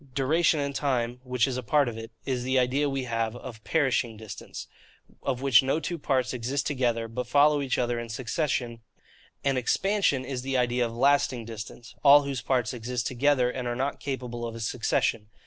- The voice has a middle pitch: No, low, 125 Hz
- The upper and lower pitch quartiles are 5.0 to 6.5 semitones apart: No, average, 2.7 semitones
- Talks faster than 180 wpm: Yes, average, 190 wpm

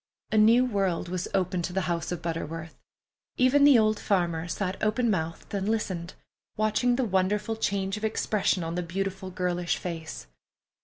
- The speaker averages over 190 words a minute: No, average, 165 wpm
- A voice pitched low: No, high, 190 Hz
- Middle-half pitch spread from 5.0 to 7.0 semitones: No, average, 3.6 semitones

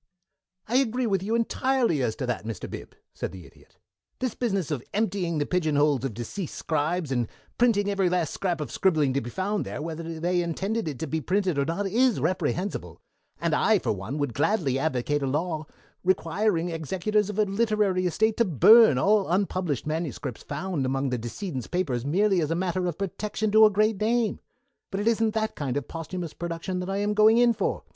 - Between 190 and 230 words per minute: Yes, average, 200 wpm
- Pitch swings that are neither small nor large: No, wide, 5.9 semitones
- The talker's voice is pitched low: No, medium, 180 Hz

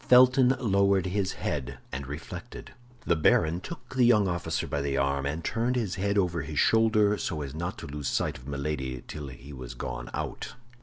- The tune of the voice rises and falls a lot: Yes, wide, 6.8 semitones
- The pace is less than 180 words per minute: No, average, 195 wpm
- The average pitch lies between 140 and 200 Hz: No, very low, 85 Hz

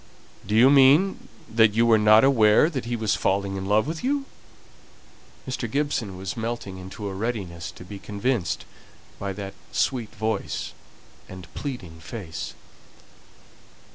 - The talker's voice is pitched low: Yes, low, 110 Hz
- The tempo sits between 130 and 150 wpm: Yes, average, 140 wpm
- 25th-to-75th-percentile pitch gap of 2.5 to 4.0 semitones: No, average, 4.4 semitones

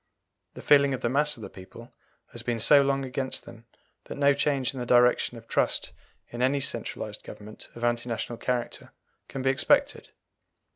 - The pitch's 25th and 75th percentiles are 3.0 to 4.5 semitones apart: No, narrow, 2.6 semitones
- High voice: No, low, 125 Hz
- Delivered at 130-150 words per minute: No, average, 185 wpm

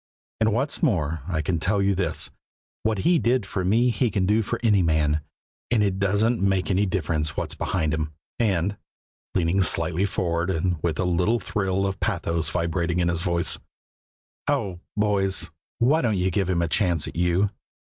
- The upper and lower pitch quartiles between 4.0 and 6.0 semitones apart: No, average, 3.4 semitones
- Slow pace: No, average, 180 wpm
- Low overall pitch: Yes, very low, 95 Hz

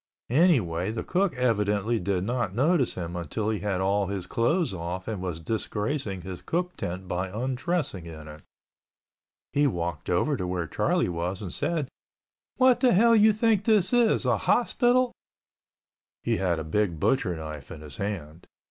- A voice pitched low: Yes, low, 100 Hz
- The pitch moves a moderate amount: No, wide, 8.9 semitones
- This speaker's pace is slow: No, average, 165 wpm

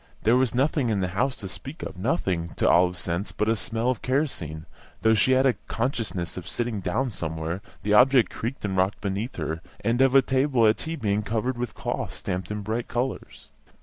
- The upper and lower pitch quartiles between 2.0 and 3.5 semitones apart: No, wide, 5.4 semitones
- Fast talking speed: Yes, fast, 215 wpm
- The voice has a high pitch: No, low, 110 Hz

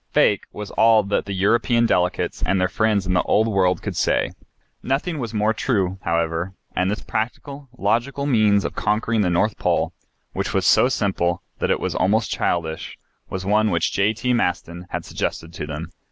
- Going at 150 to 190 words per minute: Yes, average, 180 wpm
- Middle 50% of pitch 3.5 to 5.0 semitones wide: Yes, average, 3.8 semitones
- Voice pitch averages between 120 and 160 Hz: No, low, 100 Hz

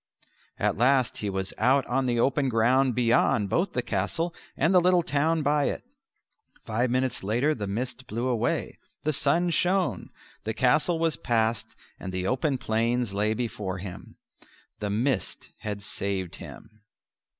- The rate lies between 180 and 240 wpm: No, average, 155 wpm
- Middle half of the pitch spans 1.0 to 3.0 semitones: No, average, 5.0 semitones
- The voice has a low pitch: Yes, low, 125 Hz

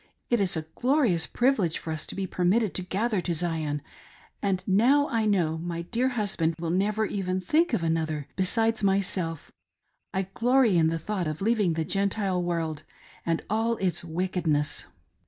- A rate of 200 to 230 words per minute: No, average, 175 wpm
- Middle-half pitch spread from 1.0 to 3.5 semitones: No, average, 4.7 semitones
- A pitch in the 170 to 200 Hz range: Yes, medium, 185 Hz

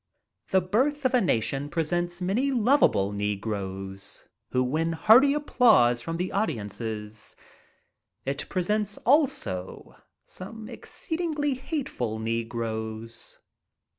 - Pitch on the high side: No, medium, 165 Hz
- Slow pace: Yes, slow, 100 wpm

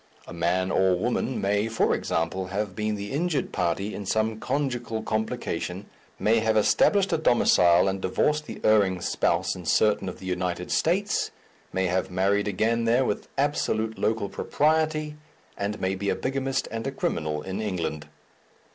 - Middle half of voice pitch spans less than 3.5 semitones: No, average, 4.6 semitones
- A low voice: Yes, low, 105 Hz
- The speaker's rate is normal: Yes, average, 165 wpm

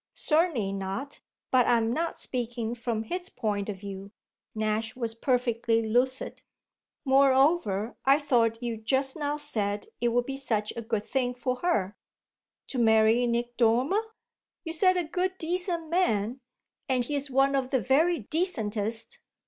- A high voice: Yes, high, 245 Hz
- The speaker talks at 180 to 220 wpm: No, average, 150 wpm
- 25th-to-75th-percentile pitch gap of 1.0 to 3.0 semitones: No, average, 4.2 semitones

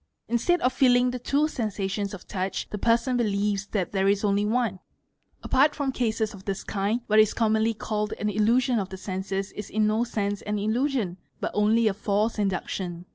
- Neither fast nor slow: Yes, average, 185 wpm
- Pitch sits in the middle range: No, high, 210 Hz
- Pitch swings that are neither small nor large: Yes, average, 3.0 semitones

